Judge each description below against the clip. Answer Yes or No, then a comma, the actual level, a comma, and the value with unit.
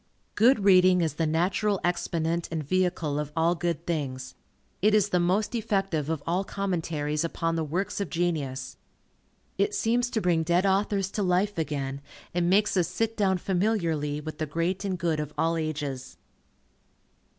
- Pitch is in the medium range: Yes, medium, 175 Hz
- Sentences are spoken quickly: No, average, 165 wpm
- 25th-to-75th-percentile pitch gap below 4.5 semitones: Yes, average, 3.8 semitones